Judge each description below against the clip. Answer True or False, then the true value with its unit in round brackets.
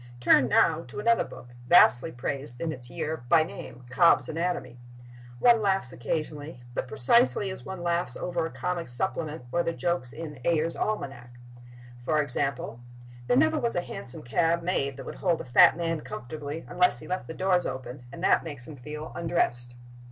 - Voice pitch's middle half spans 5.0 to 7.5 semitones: True (5.6 semitones)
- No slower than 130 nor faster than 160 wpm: False (175 wpm)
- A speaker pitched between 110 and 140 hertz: False (155 Hz)